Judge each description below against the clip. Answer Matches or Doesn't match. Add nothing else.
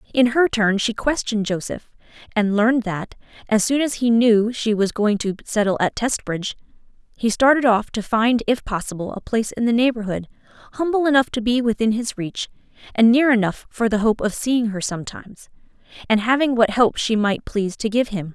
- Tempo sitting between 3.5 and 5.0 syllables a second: Doesn't match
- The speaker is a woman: Matches